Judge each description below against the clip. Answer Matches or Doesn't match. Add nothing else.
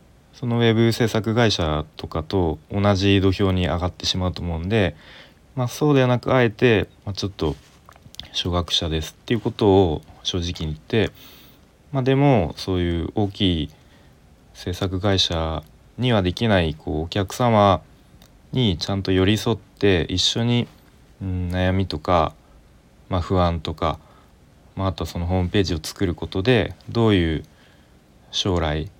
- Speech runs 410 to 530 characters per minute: Doesn't match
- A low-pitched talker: Matches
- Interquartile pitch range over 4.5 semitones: Doesn't match